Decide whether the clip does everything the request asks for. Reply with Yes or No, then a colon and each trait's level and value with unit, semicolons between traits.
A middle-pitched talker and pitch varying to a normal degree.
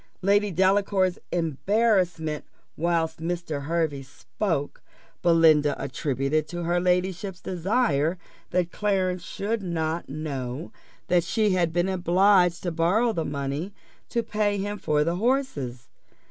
Yes: medium, 175 Hz; average, 3.6 semitones